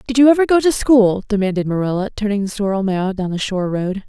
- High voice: Yes, high, 210 Hz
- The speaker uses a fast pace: Yes, fast, 235 wpm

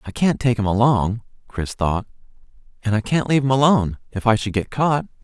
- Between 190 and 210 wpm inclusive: Yes, fast, 205 wpm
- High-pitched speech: No, low, 115 Hz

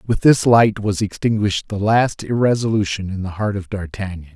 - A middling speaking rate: Yes, average, 180 wpm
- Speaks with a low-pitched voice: Yes, low, 100 Hz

